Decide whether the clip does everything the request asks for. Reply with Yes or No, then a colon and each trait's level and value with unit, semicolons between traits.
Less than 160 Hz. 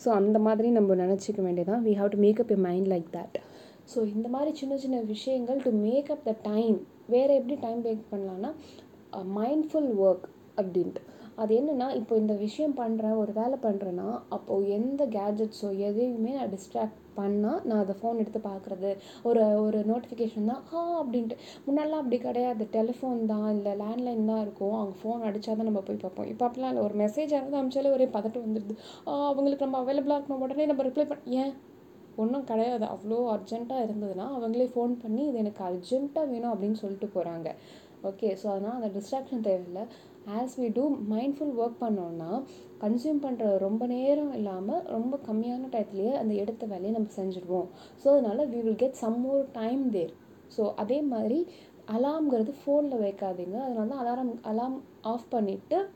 No: high, 225 Hz